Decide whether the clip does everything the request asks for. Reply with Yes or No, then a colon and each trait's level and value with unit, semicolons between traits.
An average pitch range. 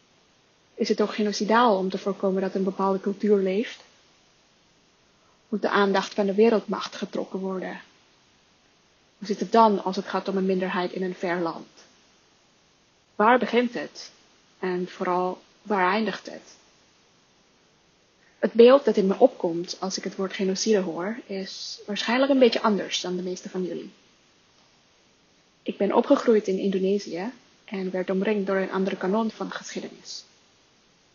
No: narrow, 2.3 semitones